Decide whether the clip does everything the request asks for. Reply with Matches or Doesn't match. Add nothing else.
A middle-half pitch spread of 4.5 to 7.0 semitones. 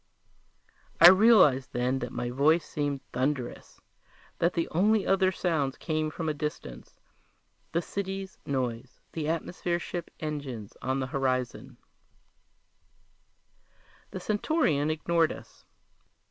Matches